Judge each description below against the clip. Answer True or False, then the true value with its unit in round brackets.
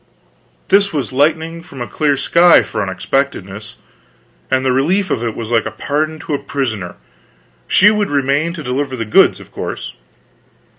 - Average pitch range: True (4.7 semitones)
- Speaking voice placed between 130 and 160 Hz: True (140 Hz)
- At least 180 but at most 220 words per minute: False (160 wpm)